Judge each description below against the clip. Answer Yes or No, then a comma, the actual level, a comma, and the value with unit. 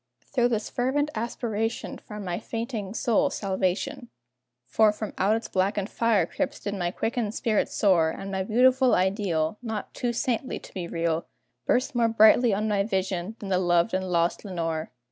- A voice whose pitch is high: Yes, high, 210 Hz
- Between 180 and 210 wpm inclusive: No, average, 170 wpm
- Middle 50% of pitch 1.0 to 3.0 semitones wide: No, average, 3.8 semitones